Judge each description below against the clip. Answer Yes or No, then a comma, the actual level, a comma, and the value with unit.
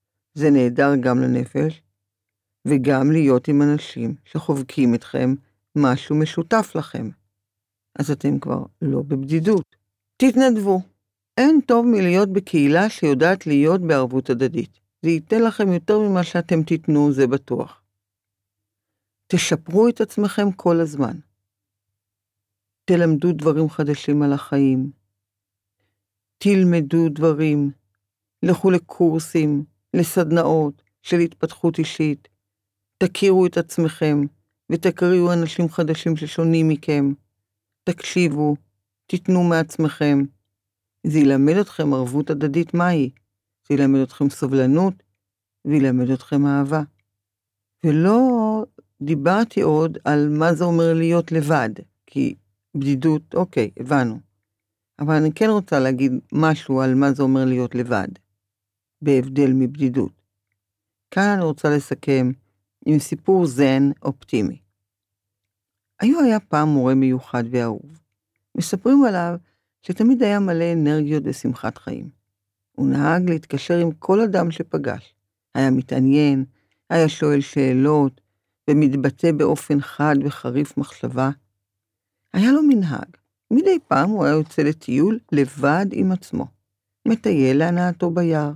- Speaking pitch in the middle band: Yes, medium, 145 Hz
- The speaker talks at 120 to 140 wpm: No, average, 110 wpm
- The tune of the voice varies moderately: No, wide, 7.7 semitones